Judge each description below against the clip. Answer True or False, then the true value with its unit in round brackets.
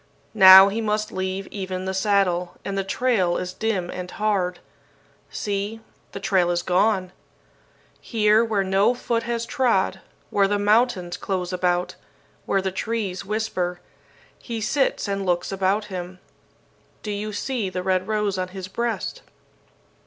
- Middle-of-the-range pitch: False (195 Hz)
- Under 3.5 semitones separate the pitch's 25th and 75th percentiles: True (2.7 semitones)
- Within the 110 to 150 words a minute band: True (145 wpm)